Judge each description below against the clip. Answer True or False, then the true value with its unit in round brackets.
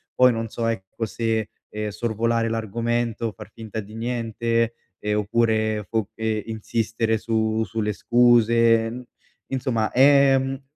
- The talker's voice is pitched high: False (115 Hz)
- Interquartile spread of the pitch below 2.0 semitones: True (1.3 semitones)